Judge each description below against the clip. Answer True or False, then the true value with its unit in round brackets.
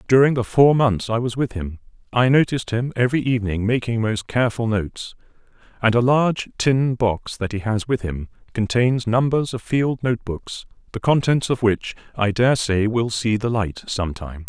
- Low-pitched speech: True (115 Hz)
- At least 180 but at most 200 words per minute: True (190 wpm)